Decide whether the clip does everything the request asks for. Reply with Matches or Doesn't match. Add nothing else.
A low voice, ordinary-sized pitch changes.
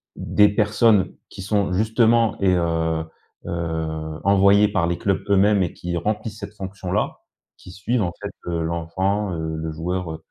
Matches